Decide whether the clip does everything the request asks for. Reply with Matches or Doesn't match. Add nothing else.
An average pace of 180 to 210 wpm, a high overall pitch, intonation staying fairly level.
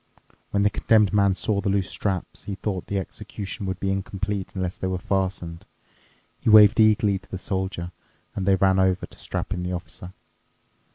Doesn't match